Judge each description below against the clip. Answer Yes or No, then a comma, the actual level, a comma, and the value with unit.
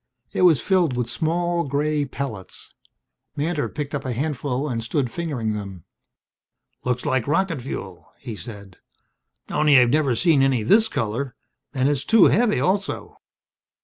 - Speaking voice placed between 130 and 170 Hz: Yes, medium, 140 Hz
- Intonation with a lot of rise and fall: No, average, 4.8 semitones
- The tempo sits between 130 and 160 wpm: Yes, average, 145 wpm